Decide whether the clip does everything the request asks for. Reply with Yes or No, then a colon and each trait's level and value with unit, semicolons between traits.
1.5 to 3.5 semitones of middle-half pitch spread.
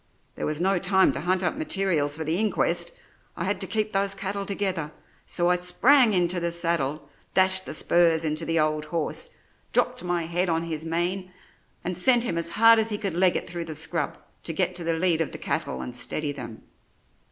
Yes: average, 2.9 semitones